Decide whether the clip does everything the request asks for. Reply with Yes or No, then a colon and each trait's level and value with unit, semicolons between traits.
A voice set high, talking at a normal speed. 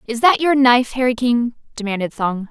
Yes: high, 240 Hz; average, 190 wpm